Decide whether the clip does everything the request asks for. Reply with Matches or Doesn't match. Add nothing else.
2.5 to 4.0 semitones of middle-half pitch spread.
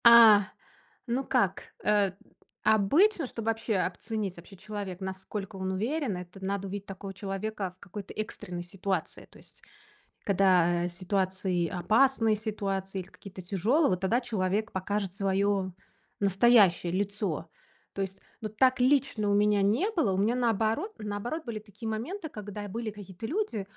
Matches